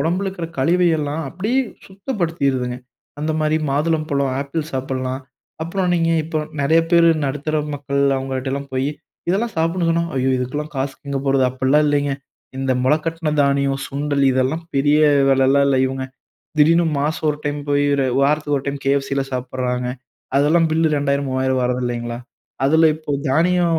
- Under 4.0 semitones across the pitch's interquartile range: Yes, average, 3.4 semitones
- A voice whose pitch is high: No, medium, 145 Hz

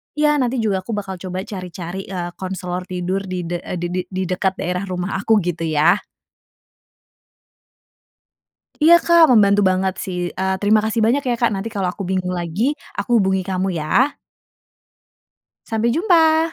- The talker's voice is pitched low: No, high, 190 Hz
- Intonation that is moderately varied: Yes, average, 3.7 semitones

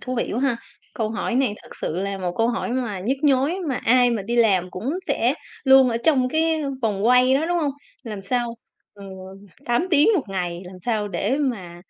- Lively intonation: No, average, 4.9 semitones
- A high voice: Yes, high, 240 Hz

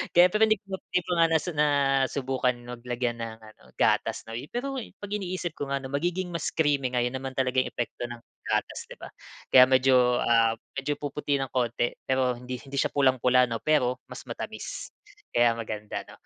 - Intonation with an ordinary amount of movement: Yes, average, 3.4 semitones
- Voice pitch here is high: No, low, 130 Hz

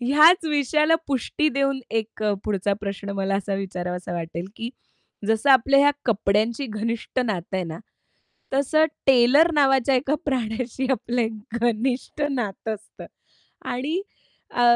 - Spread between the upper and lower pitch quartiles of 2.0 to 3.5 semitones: No, average, 5.0 semitones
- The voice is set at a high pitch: Yes, high, 240 Hz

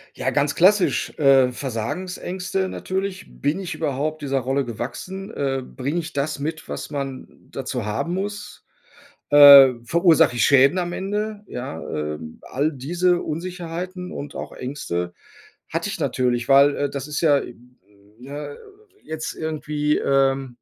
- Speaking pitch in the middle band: Yes, medium, 145 Hz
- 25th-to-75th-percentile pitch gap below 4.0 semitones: No, average, 4.7 semitones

